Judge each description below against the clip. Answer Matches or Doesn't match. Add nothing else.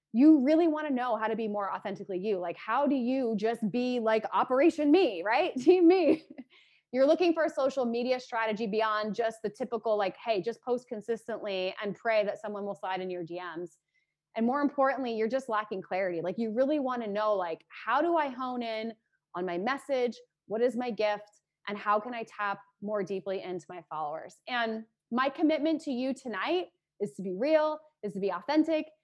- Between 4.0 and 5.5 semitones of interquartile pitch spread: Matches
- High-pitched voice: Matches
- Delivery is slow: Doesn't match